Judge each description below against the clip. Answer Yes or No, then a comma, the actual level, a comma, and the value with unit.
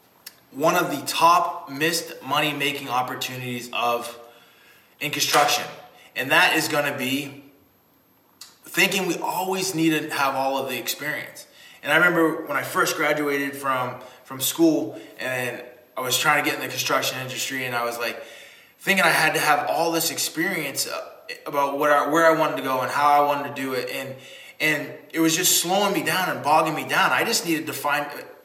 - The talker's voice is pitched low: No, medium, 145 Hz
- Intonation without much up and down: No, average, 3.2 semitones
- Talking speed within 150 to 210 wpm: Yes, average, 190 wpm